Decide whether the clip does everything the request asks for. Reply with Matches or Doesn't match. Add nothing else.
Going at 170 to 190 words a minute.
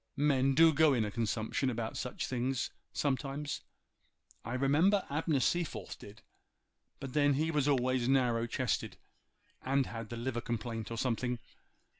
Doesn't match